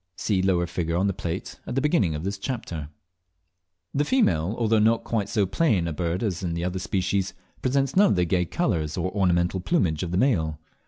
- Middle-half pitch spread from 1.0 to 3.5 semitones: No, average, 4.5 semitones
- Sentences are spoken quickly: Yes, fast, 210 wpm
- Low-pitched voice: Yes, very low, 95 Hz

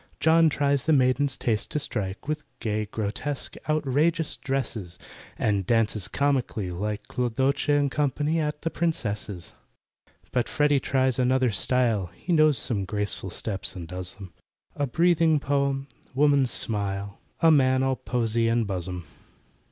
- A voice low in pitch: Yes, low, 130 Hz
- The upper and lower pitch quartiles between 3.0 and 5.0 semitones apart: No, wide, 5.5 semitones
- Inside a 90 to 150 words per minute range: Yes, slow, 135 wpm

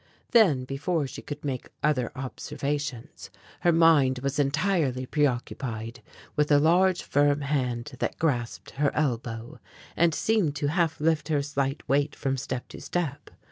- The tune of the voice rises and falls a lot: No, average, 3.3 semitones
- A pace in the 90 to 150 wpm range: Yes, average, 145 wpm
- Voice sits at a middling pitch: Yes, medium, 145 Hz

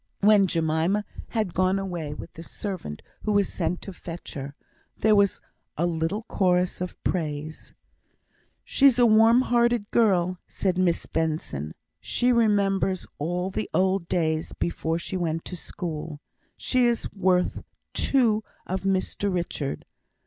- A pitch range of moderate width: Yes, average, 3.9 semitones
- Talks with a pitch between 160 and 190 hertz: Yes, medium, 185 Hz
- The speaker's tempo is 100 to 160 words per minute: Yes, average, 140 wpm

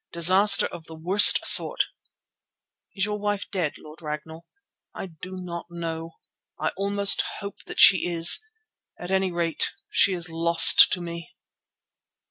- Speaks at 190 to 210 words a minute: No, average, 140 wpm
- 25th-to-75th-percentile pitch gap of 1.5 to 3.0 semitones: Yes, average, 2.7 semitones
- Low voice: No, medium, 175 Hz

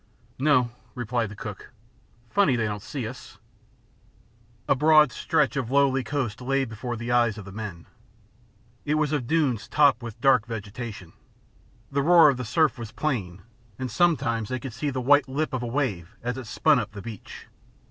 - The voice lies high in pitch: No, low, 125 Hz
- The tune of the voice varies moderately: Yes, average, 4.0 semitones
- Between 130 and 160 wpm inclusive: No, average, 180 wpm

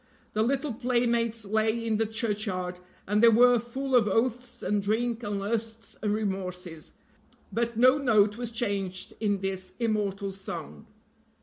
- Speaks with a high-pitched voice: Yes, high, 220 Hz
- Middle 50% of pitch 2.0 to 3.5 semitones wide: Yes, average, 2.9 semitones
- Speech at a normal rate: Yes, average, 145 wpm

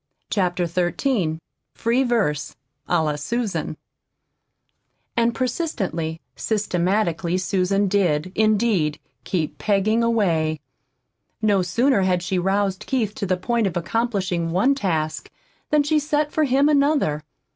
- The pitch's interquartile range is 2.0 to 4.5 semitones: No, average, 5.1 semitones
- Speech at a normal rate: No, slow, 120 wpm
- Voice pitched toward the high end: Yes, high, 195 Hz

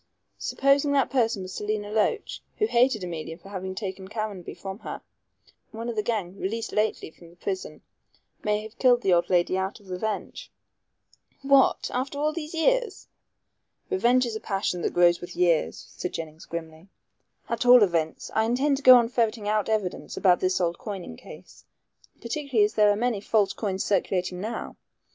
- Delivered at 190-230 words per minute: No, average, 175 wpm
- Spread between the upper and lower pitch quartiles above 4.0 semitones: Yes, average, 4.7 semitones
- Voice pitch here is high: Yes, high, 210 Hz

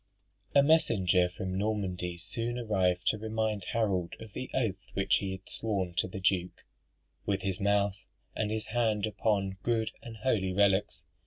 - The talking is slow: No, average, 160 wpm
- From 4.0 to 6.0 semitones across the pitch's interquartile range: No, average, 2.8 semitones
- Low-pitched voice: Yes, low, 100 Hz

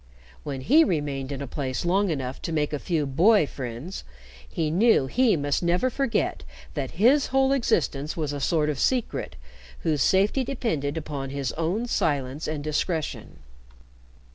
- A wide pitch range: Yes, wide, 6.8 semitones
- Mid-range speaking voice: Yes, medium, 155 Hz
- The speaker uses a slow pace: No, average, 160 wpm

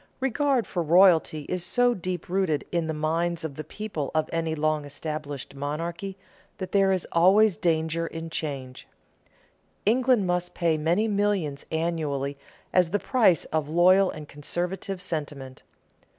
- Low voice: No, medium, 170 Hz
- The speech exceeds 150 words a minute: No, average, 145 wpm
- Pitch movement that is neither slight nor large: Yes, average, 3.7 semitones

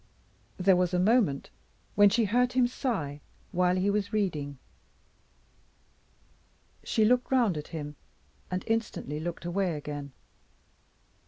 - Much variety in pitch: Yes, wide, 6.2 semitones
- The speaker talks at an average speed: No, slow, 120 wpm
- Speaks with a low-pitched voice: No, medium, 185 Hz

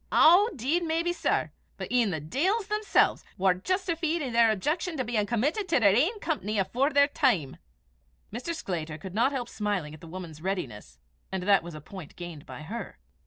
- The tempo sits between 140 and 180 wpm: No, average, 190 wpm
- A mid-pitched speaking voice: No, high, 230 Hz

